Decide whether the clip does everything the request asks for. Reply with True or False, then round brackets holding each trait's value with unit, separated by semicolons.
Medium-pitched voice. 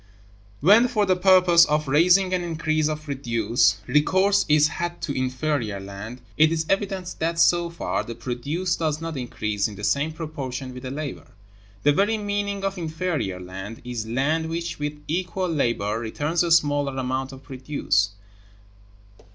True (150 Hz)